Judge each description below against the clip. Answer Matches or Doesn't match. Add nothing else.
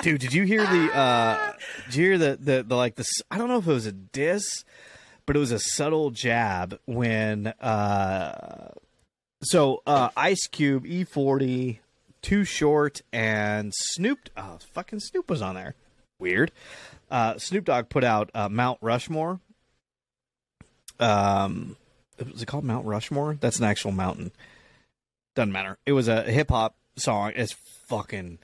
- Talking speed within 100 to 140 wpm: Doesn't match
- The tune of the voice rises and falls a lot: Matches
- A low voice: Matches